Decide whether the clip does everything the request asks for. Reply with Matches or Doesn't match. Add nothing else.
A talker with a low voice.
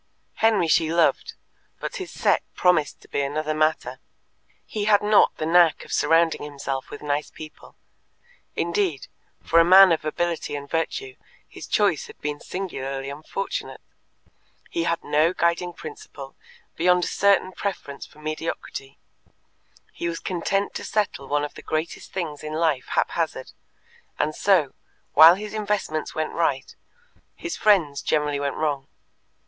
Doesn't match